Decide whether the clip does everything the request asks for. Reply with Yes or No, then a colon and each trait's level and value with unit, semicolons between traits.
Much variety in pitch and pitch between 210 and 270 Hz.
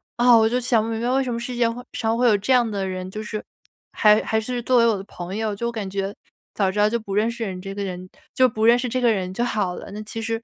No: average, 2.9 semitones; high, 220 Hz